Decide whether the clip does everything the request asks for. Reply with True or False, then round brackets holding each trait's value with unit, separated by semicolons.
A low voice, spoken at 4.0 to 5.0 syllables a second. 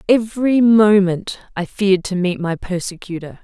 False (195 Hz; 4.8 syllables/s)